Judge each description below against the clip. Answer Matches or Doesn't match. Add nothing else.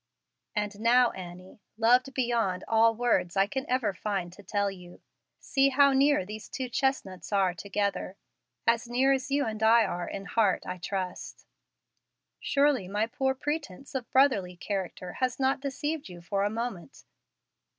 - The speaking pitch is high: Matches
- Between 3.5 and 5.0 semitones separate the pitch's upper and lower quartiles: Doesn't match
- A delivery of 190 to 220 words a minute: Doesn't match